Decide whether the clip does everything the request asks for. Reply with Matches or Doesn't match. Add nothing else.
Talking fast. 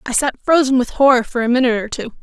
Matches